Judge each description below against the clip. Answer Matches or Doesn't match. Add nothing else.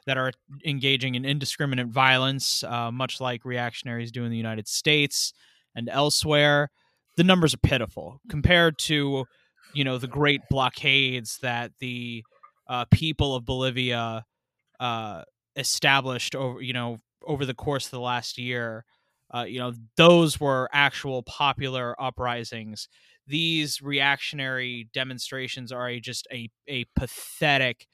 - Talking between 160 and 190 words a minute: Doesn't match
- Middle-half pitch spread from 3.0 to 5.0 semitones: Doesn't match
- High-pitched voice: Doesn't match